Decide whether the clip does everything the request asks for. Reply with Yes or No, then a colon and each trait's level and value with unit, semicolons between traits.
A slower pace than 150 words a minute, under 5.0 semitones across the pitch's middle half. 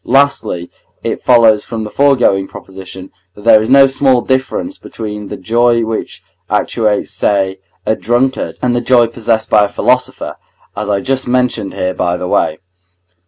No: average, 165 wpm; average, 3.8 semitones